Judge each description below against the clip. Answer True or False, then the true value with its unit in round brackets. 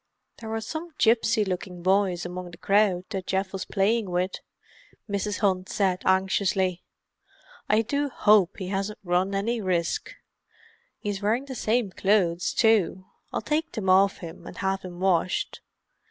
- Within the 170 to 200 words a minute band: False (155 wpm)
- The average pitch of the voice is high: True (195 Hz)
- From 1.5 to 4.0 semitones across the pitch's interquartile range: True (2.7 semitones)